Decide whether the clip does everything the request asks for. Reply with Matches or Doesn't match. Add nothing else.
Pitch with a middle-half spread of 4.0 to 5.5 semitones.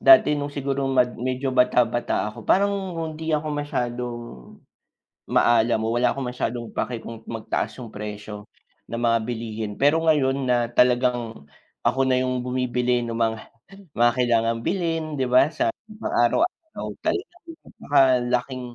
Doesn't match